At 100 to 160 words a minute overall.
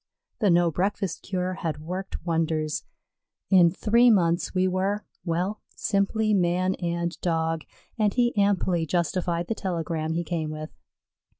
Yes: slow, 135 wpm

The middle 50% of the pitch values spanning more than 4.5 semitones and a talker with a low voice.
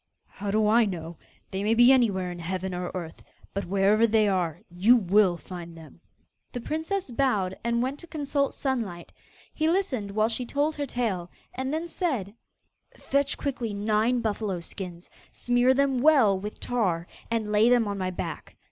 No: wide, 5.4 semitones; high, 215 Hz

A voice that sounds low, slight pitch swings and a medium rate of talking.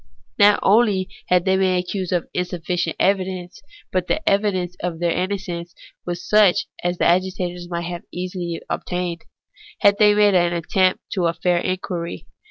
No: medium, 180 Hz; narrow, 1.6 semitones; average, 150 wpm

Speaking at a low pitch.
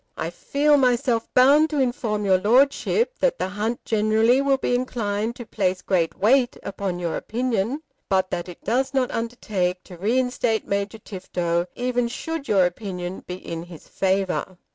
No: high, 220 Hz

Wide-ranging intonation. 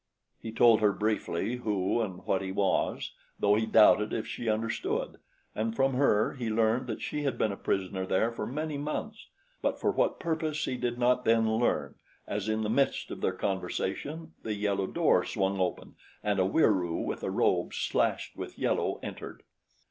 No: average, 4.0 semitones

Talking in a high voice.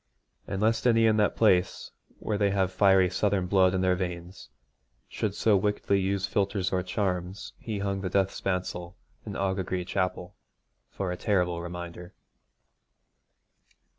No: very low, 95 Hz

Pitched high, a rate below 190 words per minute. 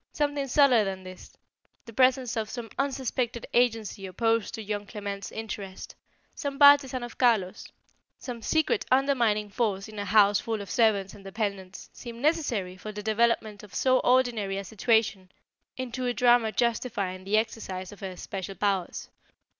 Yes: high, 220 Hz; average, 155 wpm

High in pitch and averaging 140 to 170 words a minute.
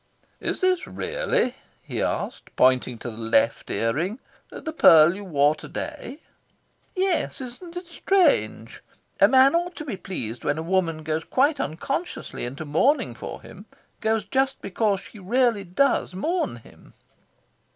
Yes: high, 205 Hz; average, 150 wpm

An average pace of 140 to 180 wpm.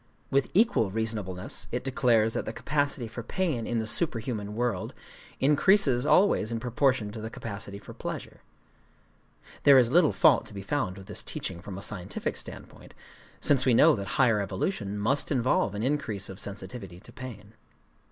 Yes: average, 165 wpm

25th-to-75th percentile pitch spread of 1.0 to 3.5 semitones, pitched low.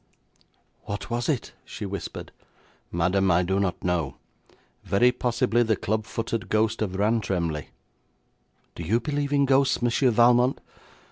No: average, 4.2 semitones; low, 110 Hz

